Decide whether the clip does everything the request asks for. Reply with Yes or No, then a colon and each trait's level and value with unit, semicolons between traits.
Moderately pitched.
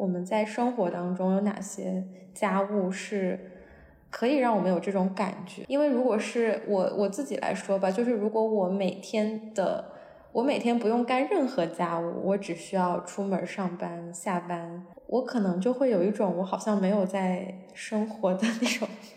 No: high, 200 Hz